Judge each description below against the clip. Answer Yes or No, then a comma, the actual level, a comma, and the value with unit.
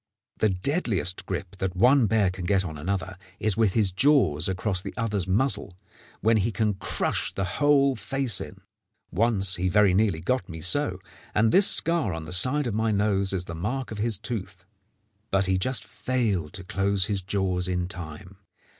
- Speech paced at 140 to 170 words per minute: No, average, 185 wpm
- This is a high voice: No, low, 100 Hz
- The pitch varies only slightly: No, average, 3.6 semitones